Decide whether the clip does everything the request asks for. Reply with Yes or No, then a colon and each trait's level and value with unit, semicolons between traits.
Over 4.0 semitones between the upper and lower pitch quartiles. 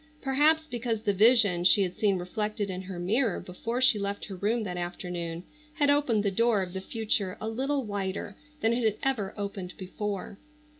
No: average, 3.7 semitones